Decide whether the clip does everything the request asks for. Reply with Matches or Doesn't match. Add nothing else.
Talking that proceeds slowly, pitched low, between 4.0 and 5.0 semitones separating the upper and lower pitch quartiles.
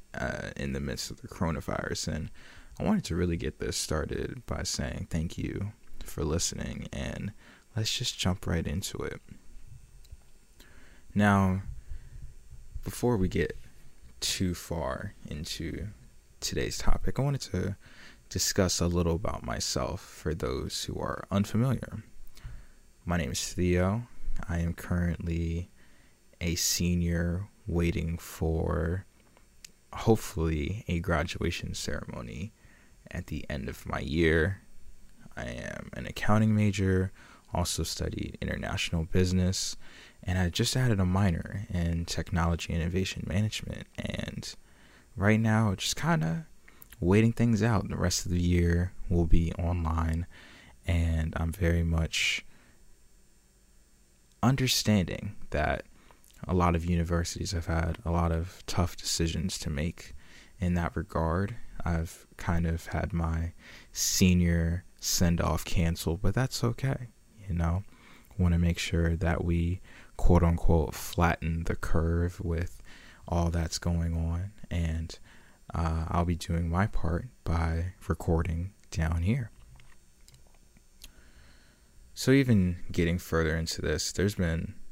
Doesn't match